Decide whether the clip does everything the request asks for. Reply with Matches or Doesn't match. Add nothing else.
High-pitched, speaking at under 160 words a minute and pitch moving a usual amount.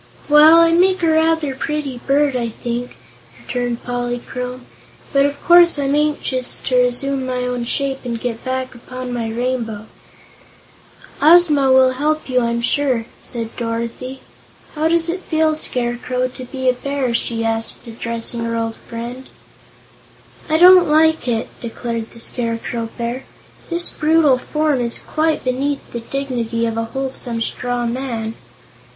Matches